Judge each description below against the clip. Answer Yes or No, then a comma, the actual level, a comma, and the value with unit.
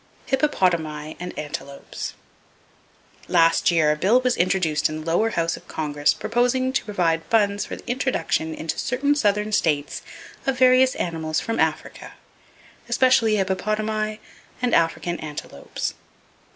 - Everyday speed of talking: No, slow, 130 wpm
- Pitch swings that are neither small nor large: No, wide, 6.7 semitones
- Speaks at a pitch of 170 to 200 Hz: Yes, high, 190 Hz